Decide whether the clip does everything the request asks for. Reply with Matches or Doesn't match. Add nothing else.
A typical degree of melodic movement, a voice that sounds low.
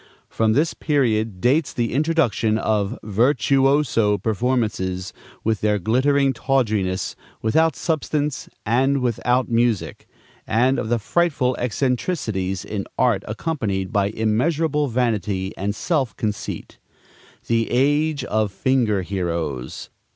Matches